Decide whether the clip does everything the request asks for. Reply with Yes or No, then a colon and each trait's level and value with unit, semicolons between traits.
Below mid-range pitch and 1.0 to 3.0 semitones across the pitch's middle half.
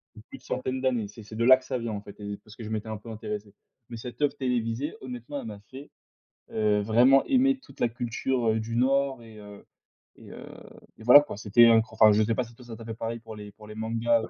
Yes: low, 115 Hz; narrow, 2.6 semitones